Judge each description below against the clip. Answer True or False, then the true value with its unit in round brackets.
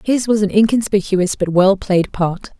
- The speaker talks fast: False (185 wpm)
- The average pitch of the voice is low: False (200 Hz)